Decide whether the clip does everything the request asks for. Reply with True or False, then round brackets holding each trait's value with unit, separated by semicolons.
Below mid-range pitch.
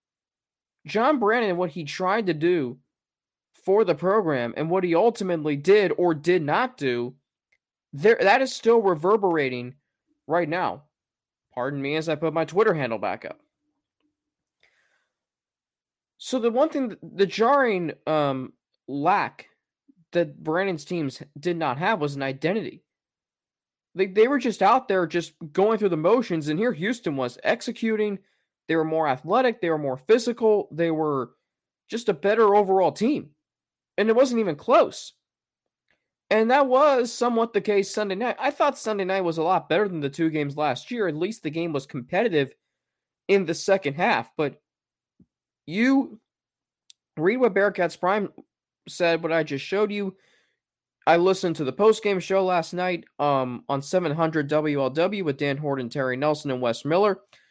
False (180 Hz)